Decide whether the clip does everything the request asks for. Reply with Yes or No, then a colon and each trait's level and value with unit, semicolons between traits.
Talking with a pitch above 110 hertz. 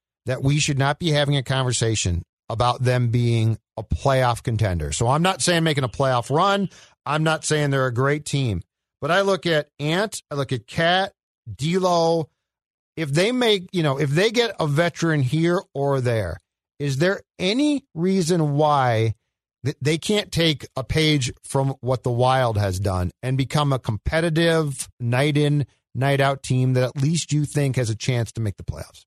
Yes: medium, 140 Hz